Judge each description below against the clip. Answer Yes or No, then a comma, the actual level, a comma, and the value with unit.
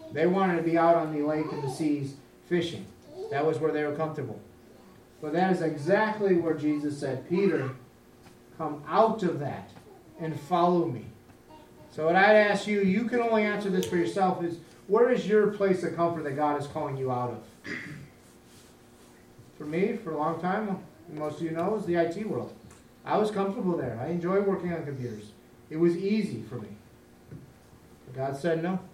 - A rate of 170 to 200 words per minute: Yes, average, 190 wpm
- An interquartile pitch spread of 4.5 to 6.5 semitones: Yes, average, 5.3 semitones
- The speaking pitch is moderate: Yes, medium, 165 Hz